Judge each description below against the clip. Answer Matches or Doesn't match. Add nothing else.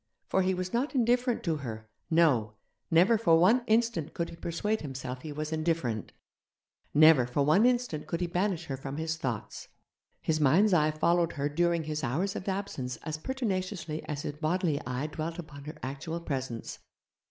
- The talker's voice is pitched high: Doesn't match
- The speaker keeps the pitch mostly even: Doesn't match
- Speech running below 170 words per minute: Doesn't match